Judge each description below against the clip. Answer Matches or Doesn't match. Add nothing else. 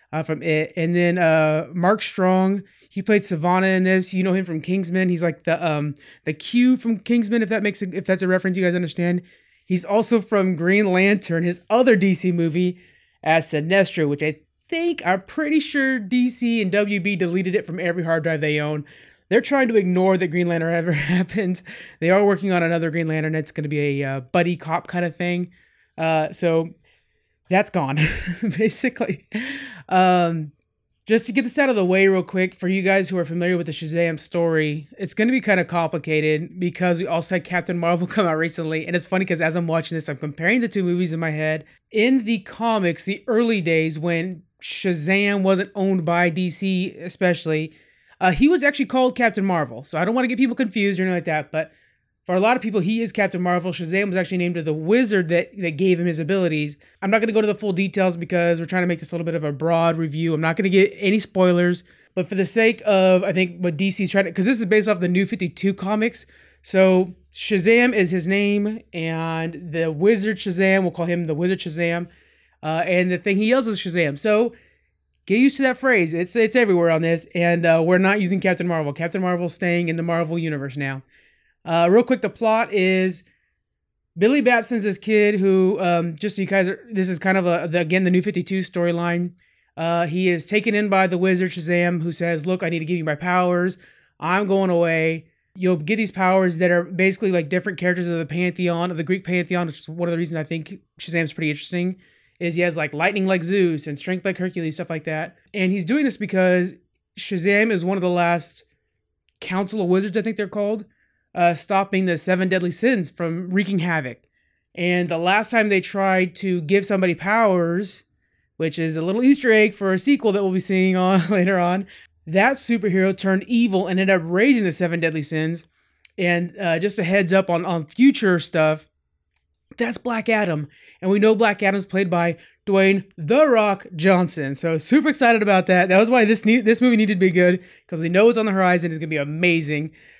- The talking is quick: Matches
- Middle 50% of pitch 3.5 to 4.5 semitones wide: Doesn't match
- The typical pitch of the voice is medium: Matches